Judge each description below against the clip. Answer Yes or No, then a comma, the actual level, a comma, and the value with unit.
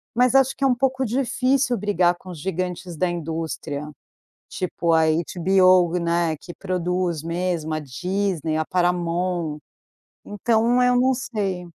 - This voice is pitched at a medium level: Yes, medium, 180 Hz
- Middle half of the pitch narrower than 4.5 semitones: No, average, 4.8 semitones